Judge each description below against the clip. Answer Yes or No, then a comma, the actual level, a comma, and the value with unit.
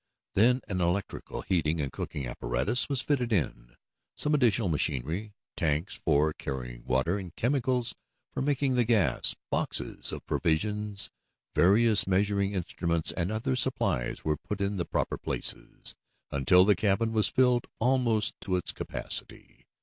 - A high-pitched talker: No, low, 100 Hz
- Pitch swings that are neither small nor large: No, wide, 6.4 semitones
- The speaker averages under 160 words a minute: Yes, average, 140 wpm